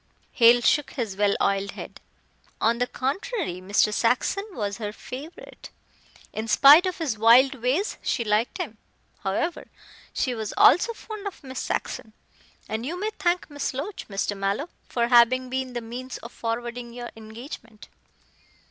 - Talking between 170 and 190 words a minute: No, average, 155 wpm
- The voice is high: Yes, high, 240 Hz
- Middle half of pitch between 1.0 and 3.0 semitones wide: No, average, 4.6 semitones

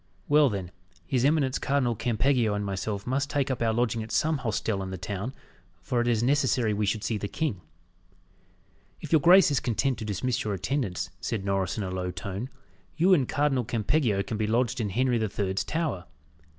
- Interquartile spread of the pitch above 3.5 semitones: Yes, average, 4.8 semitones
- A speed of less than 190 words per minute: No, average, 200 wpm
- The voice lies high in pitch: No, low, 115 Hz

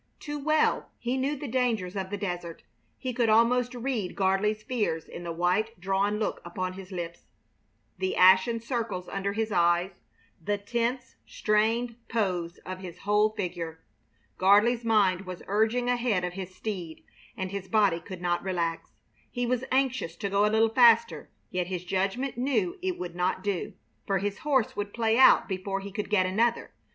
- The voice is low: No, high, 205 Hz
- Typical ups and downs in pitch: Yes, average, 4.2 semitones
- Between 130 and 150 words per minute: No, average, 175 wpm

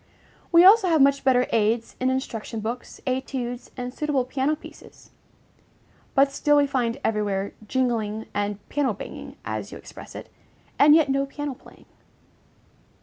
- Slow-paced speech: No, average, 145 wpm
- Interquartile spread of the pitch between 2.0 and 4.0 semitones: Yes, average, 3.7 semitones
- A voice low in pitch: No, very high, 260 Hz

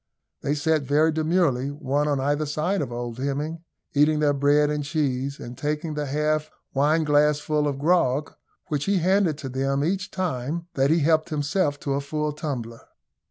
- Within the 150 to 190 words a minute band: Yes, average, 170 wpm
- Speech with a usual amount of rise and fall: No, narrow, 2.0 semitones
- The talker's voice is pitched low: No, medium, 150 Hz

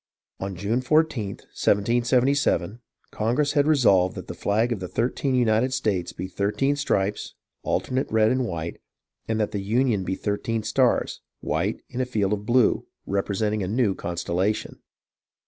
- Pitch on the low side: Yes, low, 110 Hz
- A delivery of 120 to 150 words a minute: Yes, average, 145 wpm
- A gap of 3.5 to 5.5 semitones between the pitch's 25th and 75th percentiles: Yes, average, 4.3 semitones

